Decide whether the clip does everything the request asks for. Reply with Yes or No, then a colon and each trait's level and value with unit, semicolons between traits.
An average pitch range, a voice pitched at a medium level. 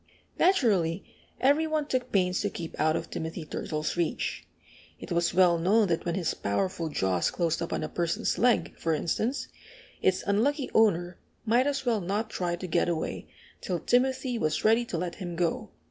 No: wide, 5.8 semitones; medium, 180 Hz